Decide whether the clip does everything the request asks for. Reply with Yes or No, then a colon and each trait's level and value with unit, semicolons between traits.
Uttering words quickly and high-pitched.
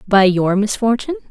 No: average, 140 wpm; high, 215 Hz